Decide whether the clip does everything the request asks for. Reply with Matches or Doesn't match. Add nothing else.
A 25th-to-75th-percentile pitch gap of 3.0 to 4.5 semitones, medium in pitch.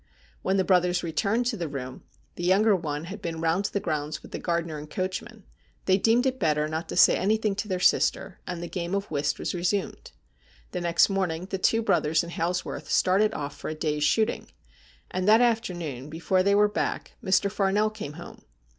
Matches